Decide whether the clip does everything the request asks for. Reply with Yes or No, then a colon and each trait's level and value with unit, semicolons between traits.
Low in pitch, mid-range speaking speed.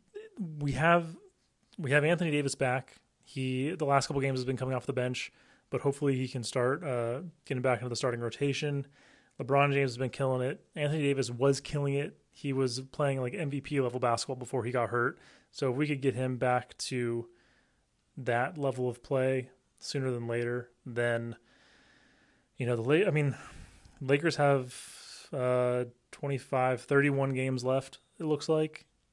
Yes: low, 130 Hz; average, 175 wpm